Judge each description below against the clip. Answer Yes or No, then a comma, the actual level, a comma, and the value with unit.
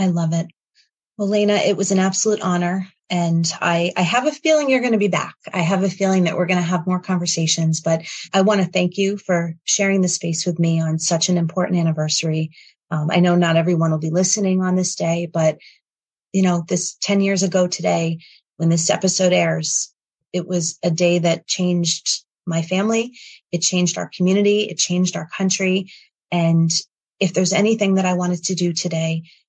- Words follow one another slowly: No, average, 200 wpm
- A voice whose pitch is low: No, medium, 180 Hz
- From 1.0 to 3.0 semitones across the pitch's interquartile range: Yes, narrow, 2.4 semitones